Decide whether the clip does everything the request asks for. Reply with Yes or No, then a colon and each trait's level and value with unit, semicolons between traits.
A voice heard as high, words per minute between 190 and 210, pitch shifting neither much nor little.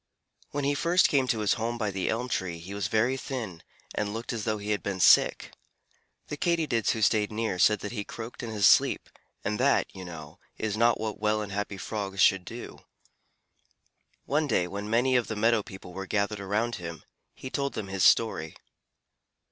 No: low, 105 Hz; average, 200 wpm; average, 3.3 semitones